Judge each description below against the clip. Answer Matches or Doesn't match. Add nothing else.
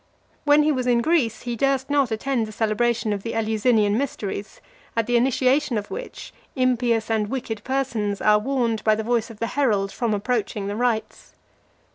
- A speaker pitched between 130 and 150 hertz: Doesn't match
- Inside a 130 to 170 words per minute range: Doesn't match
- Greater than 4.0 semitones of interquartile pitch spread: Doesn't match